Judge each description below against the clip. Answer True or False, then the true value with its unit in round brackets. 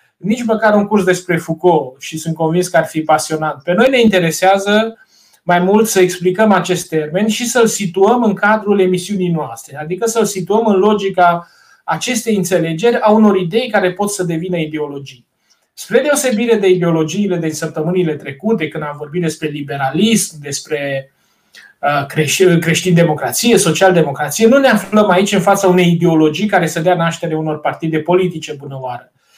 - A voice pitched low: False (180 Hz)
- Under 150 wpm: False (155 wpm)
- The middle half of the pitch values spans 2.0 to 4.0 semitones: False (4.7 semitones)